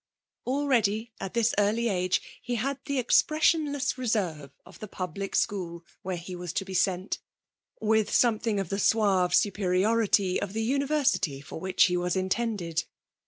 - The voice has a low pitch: No, high, 205 Hz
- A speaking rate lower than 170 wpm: Yes, average, 155 wpm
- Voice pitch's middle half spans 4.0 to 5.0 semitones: Yes, average, 4.3 semitones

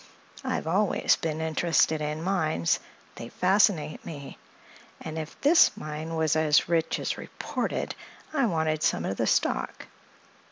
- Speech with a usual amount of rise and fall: No, narrow, 2.3 semitones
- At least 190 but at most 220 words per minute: No, slow, 135 wpm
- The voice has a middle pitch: Yes, medium, 160 Hz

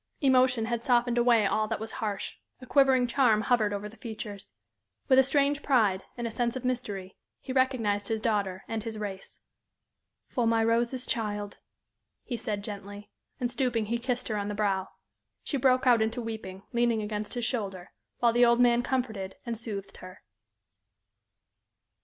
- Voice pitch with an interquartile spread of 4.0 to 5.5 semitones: No, average, 3.0 semitones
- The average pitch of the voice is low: No, high, 230 Hz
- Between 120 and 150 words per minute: No, average, 170 wpm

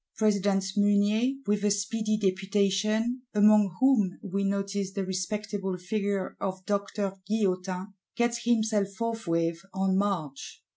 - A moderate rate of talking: No, slow, 115 wpm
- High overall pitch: Yes, high, 200 Hz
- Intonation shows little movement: Yes, narrow, 1.9 semitones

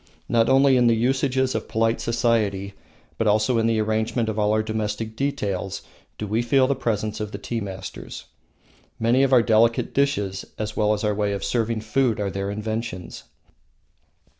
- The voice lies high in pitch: No, low, 110 Hz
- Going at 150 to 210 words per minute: Yes, average, 180 wpm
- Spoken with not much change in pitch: Yes, narrow, 2.1 semitones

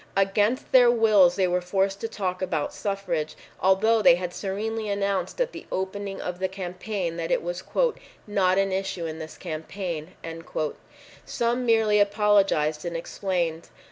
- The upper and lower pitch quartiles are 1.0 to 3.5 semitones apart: Yes, average, 2.8 semitones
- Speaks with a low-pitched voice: No, high, 195 Hz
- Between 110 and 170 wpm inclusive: Yes, average, 150 wpm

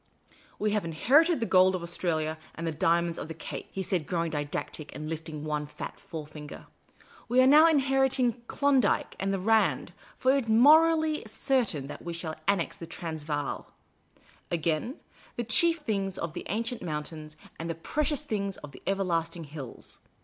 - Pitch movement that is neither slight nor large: No, wide, 7.6 semitones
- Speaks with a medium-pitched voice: Yes, medium, 180 Hz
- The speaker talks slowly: No, average, 180 wpm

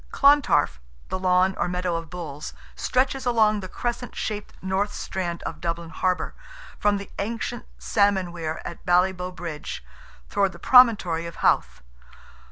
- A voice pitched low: No, medium, 185 Hz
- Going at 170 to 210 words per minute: No, average, 145 wpm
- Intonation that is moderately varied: Yes, average, 3.4 semitones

